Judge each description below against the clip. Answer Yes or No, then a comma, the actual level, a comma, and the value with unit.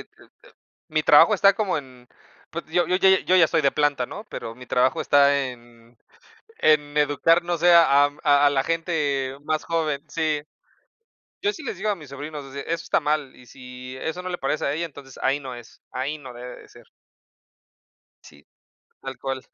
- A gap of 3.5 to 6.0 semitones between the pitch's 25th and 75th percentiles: Yes, average, 3.8 semitones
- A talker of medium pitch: Yes, medium, 145 Hz